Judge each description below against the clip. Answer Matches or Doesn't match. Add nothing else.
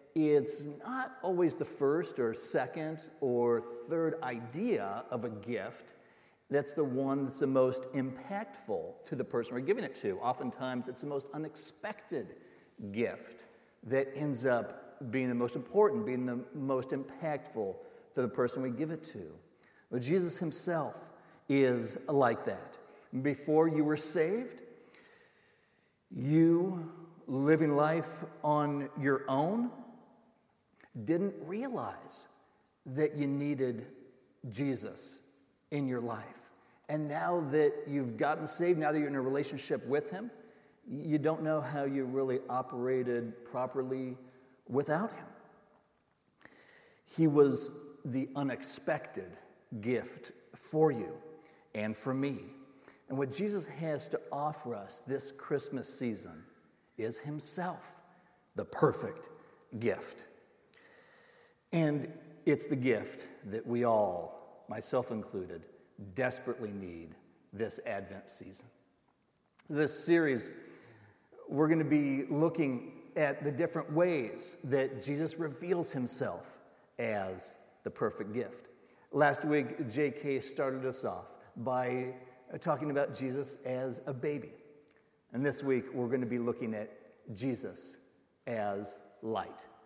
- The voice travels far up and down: Doesn't match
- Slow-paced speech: Matches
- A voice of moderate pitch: Matches